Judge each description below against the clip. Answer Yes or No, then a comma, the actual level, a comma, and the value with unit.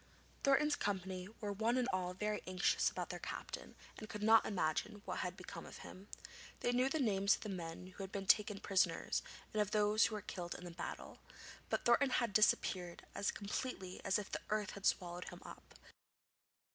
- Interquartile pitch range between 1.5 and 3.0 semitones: Yes, average, 2.7 semitones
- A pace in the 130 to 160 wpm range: No, average, 195 wpm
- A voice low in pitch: No, high, 205 Hz